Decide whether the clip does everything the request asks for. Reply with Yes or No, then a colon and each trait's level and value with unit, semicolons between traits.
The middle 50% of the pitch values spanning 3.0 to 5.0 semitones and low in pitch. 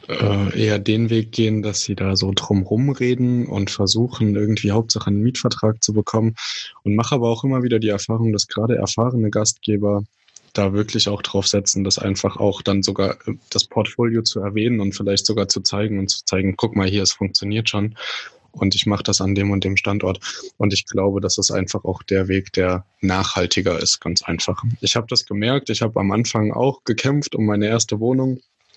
No: narrow, 2.5 semitones; low, 105 Hz